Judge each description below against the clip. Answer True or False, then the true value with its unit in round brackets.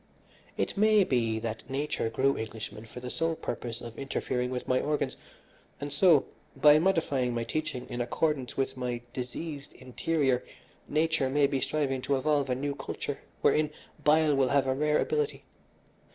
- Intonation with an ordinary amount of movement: True (3.4 semitones)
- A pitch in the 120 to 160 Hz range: True (140 Hz)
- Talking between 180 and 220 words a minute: False (165 wpm)